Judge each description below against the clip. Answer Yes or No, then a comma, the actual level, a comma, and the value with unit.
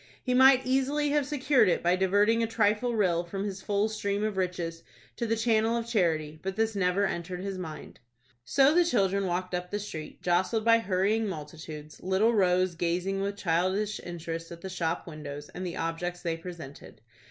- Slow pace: No, average, 185 wpm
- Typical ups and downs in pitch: Yes, average, 4.3 semitones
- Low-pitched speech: No, high, 190 Hz